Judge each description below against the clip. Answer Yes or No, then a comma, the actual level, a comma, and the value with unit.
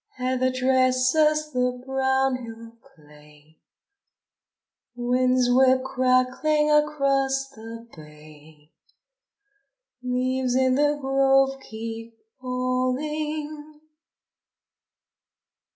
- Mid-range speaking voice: No, very high, 255 Hz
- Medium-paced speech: No, slow, 70 wpm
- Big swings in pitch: No, narrow, 1.8 semitones